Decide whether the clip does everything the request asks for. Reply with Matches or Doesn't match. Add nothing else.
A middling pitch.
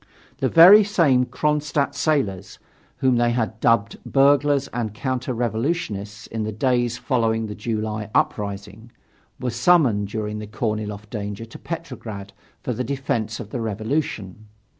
Doesn't match